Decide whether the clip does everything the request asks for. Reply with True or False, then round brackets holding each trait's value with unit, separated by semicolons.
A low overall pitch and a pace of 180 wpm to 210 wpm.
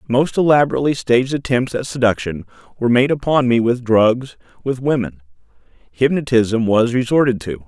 False (120 Hz; 140 wpm)